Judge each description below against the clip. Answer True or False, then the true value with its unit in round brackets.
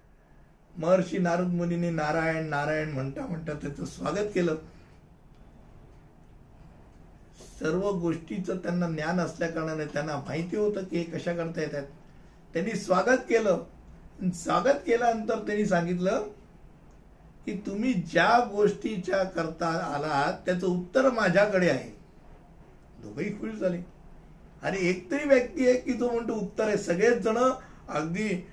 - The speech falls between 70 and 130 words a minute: True (120 wpm)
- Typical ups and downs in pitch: True (4.1 semitones)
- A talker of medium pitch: True (180 Hz)